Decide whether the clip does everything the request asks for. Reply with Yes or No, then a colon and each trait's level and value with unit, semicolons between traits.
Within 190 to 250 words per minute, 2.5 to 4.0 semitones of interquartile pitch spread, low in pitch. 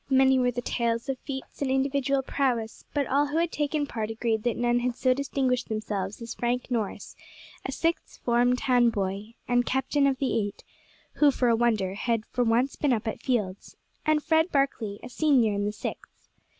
No: average, 195 wpm; average, 3.3 semitones; high, 245 Hz